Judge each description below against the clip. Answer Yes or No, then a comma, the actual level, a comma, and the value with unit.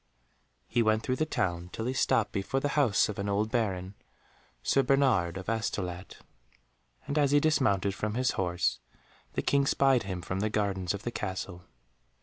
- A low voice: Yes, low, 105 Hz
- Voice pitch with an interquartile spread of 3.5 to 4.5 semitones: No, average, 5.3 semitones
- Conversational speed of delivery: Yes, average, 175 wpm